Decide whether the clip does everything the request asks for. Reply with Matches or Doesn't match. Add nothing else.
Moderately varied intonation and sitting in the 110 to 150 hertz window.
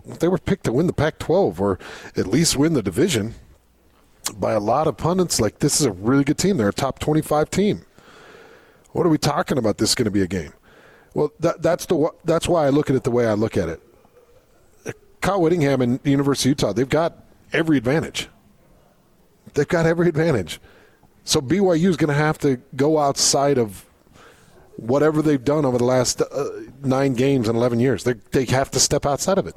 Matches